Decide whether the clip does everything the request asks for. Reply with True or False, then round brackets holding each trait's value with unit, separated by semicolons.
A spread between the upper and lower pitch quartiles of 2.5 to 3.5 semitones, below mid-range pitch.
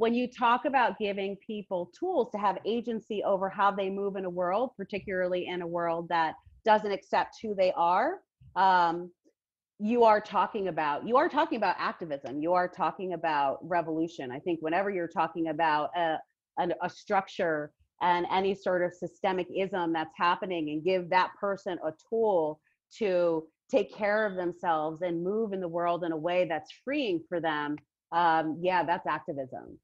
False (3.1 semitones; 180 Hz)